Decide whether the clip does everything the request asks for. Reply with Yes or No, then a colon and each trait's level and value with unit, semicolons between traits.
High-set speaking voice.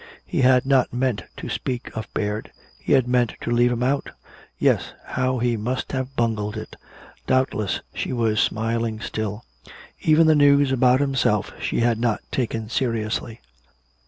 No: low, 120 Hz